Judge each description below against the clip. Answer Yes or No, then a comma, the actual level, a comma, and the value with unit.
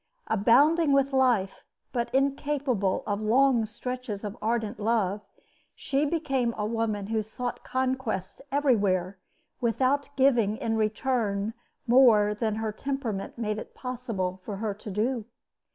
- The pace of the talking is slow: Yes, slow, 130 wpm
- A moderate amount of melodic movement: Yes, average, 3.9 semitones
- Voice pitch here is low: No, high, 230 Hz